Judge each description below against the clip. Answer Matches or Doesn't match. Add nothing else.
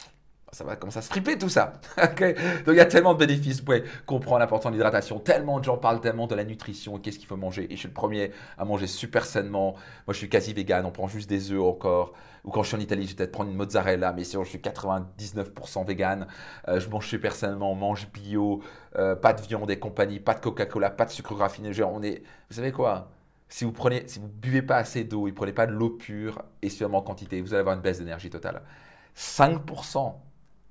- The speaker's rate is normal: Doesn't match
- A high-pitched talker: Doesn't match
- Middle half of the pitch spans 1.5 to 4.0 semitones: Matches